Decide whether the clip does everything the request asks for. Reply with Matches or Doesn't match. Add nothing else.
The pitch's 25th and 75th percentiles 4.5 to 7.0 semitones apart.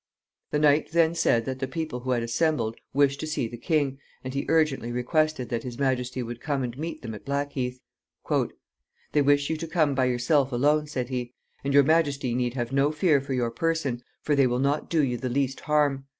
Doesn't match